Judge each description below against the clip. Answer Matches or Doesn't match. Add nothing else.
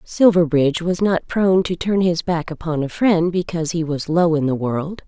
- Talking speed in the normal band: Doesn't match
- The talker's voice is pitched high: Doesn't match